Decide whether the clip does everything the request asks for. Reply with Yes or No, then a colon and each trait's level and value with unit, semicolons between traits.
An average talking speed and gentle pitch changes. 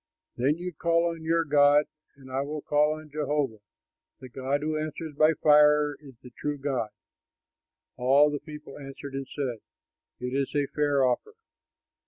Yes: average, 165 wpm; narrow, 2.0 semitones